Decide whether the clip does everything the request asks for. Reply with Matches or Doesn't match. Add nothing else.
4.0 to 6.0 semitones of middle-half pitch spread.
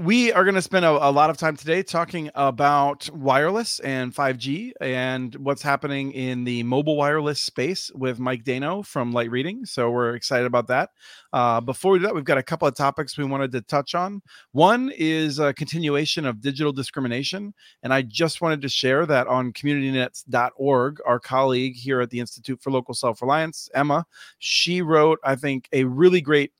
Doesn't match